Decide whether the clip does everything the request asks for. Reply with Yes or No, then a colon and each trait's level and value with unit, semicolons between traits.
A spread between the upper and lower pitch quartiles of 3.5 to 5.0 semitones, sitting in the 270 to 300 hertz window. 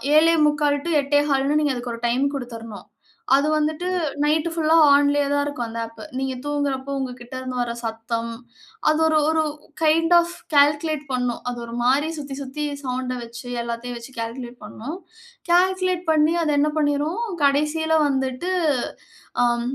Yes: average, 3.8 semitones; very high, 280 Hz